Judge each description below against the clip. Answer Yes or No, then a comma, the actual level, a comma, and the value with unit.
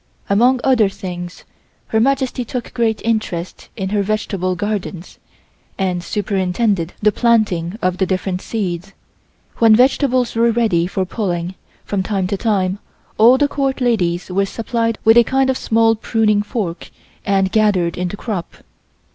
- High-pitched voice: Yes, high, 210 Hz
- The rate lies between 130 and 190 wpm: Yes, average, 150 wpm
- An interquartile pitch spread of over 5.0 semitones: No, average, 3.8 semitones